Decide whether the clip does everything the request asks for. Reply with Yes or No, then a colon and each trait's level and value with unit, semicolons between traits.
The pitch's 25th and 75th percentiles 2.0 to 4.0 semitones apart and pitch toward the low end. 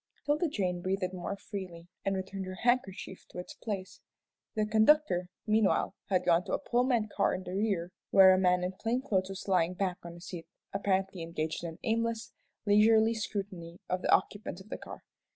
No: average, 3.2 semitones; high, 190 Hz